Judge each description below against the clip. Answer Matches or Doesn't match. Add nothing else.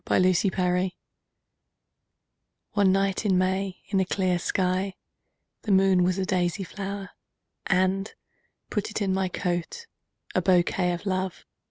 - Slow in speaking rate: Matches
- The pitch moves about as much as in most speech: Doesn't match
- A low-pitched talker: Doesn't match